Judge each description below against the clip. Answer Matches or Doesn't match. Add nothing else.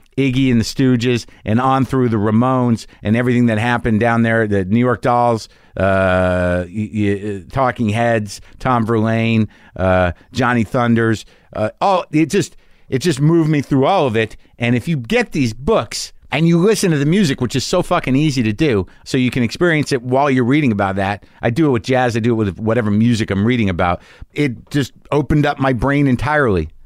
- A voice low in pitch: Matches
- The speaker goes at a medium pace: Matches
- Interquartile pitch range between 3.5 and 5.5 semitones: Matches